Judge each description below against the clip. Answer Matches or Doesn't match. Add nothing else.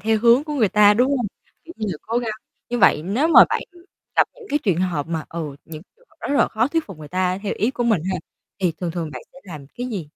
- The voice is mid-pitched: Doesn't match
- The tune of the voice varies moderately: Doesn't match